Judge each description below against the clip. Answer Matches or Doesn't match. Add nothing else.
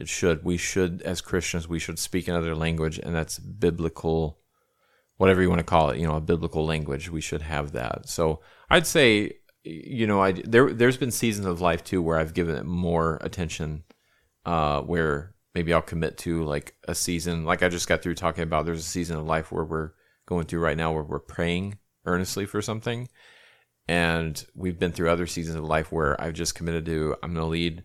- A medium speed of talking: Doesn't match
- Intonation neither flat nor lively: Doesn't match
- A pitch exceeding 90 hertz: Doesn't match